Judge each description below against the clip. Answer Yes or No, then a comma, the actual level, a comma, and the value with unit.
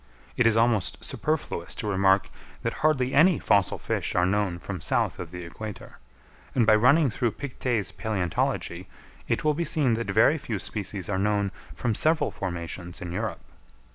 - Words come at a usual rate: Yes, average, 170 wpm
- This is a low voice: Yes, low, 105 Hz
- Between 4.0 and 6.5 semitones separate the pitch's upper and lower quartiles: Yes, average, 5.0 semitones